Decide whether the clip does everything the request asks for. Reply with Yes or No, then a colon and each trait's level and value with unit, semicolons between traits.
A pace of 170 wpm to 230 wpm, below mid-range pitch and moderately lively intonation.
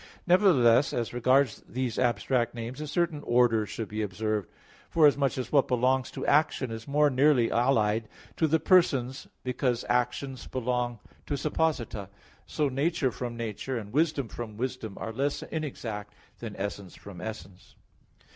No: average, 145 wpm; low, 125 Hz; average, 3.9 semitones